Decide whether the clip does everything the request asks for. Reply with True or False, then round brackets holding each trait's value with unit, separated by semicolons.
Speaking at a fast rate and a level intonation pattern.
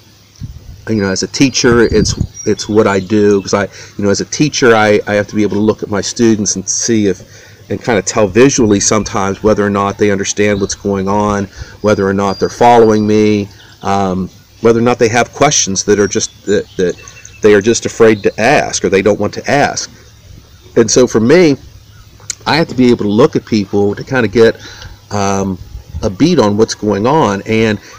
True (215 wpm; 1.9 semitones)